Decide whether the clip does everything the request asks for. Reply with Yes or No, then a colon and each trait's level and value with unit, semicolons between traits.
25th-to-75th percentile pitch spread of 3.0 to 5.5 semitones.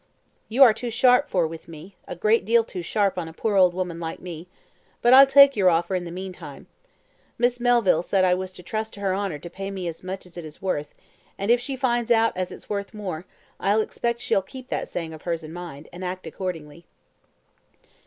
Yes: average, 4.5 semitones